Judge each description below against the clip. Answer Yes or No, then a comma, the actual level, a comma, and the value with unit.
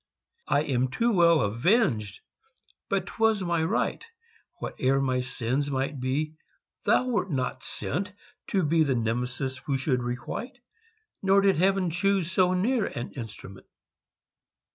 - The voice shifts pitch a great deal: Yes, wide, 7.0 semitones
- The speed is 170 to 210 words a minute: No, slow, 135 wpm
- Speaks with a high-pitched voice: No, medium, 145 Hz